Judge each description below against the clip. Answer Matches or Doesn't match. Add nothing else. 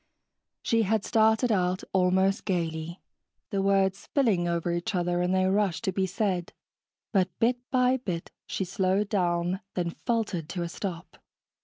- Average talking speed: Matches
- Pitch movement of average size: Matches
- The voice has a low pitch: Doesn't match